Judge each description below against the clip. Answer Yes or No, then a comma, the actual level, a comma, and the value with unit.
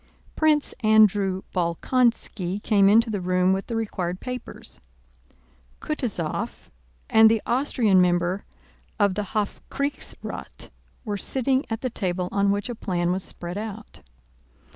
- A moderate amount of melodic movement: Yes, average, 3.6 semitones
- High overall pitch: Yes, high, 205 Hz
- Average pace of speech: No, slow, 125 wpm